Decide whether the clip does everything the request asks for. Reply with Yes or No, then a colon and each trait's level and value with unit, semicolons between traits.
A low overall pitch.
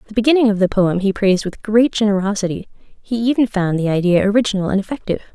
No: high, 205 Hz